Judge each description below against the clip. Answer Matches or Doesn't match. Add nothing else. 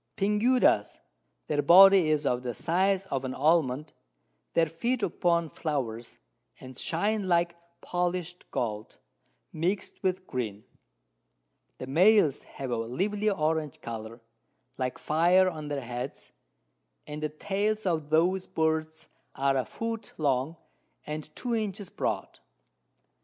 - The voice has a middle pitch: Matches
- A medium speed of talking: Doesn't match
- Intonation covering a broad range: Matches